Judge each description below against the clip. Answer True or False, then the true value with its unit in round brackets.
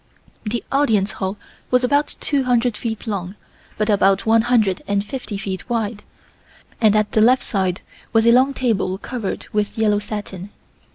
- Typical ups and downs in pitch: True (3.2 semitones)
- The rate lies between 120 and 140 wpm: False (165 wpm)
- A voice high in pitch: True (215 Hz)